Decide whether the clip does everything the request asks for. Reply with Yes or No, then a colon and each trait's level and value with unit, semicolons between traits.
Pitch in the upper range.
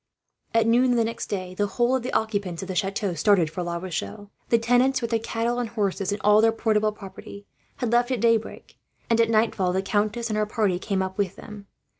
Yes: high, 215 Hz